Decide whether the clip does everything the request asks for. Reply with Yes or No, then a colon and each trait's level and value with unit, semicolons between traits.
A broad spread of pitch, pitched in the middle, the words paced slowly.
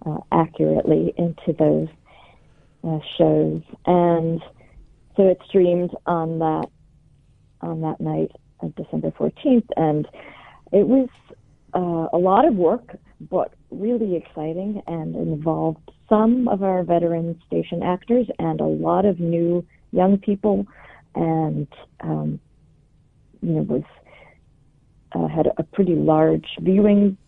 No: average, 4.1 semitones; medium, 165 Hz; slow, 115 wpm